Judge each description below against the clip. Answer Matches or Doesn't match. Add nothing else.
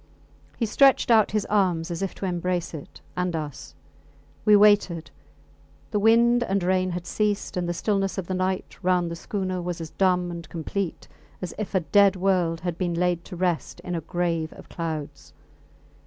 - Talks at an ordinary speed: Matches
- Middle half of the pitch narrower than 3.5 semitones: Matches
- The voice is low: Doesn't match